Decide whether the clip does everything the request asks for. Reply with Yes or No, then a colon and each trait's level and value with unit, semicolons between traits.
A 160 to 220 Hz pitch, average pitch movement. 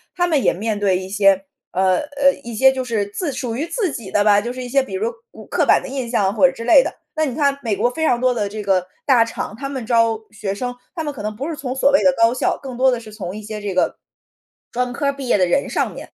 No: high, 240 Hz; average, 4.8 semitones